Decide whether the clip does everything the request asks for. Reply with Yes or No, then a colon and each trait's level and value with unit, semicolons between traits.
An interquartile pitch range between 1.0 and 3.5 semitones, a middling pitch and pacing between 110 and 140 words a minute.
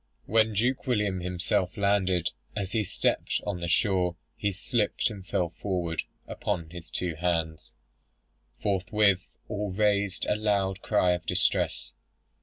No: average, 2.8 semitones; very low, 95 Hz; slow, 135 wpm